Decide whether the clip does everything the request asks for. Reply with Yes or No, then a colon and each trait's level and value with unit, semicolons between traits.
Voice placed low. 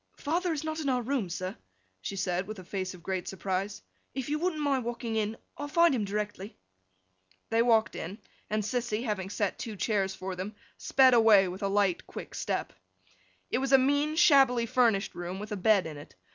No: high, 215 Hz